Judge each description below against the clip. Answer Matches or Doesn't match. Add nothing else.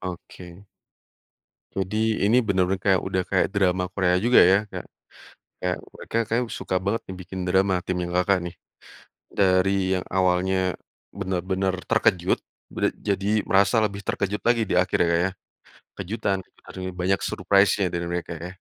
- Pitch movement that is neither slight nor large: Doesn't match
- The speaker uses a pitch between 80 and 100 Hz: Matches